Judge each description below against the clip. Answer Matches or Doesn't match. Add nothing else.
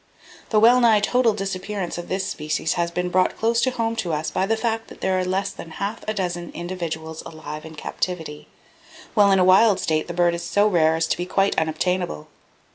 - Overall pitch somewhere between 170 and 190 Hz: Matches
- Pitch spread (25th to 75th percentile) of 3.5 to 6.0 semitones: Matches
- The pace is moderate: Doesn't match